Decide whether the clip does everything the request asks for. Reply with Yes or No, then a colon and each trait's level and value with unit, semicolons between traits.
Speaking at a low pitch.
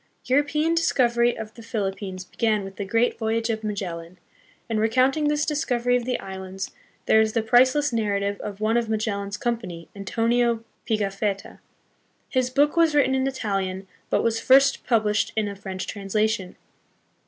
No: high, 220 Hz